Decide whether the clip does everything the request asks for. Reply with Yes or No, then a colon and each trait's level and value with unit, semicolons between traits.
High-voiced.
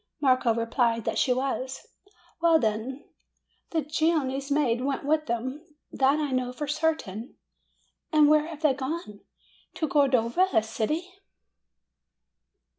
Yes: very high, 275 Hz